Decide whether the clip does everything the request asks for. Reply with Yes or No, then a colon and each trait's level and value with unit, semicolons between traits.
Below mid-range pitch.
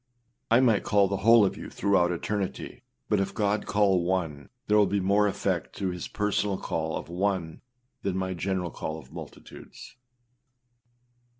Yes: very low, 95 Hz